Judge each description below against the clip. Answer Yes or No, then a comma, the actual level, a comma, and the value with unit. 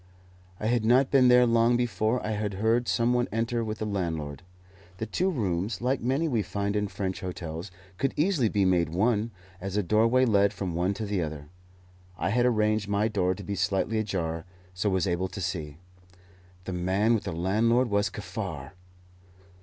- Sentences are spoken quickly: No, average, 185 wpm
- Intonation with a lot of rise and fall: No, average, 3.8 semitones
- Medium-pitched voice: No, low, 105 Hz